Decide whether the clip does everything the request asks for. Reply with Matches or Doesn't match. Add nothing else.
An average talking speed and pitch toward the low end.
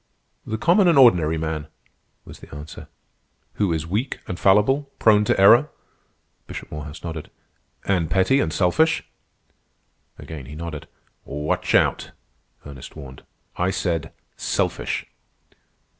Doesn't match